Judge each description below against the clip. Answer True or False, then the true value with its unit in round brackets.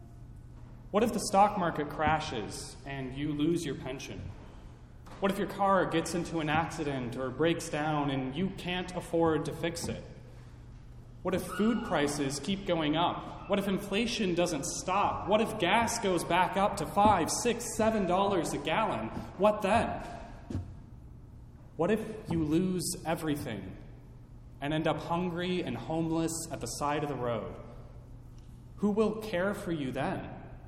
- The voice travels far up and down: True (5.9 semitones)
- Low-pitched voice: False (165 Hz)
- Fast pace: False (155 wpm)